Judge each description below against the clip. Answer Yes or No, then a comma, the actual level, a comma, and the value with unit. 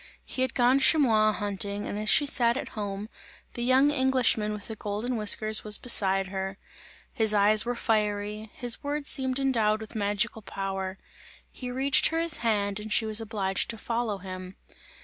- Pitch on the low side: No, high, 215 Hz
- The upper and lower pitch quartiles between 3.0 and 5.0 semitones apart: Yes, average, 3.3 semitones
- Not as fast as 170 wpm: No, average, 175 wpm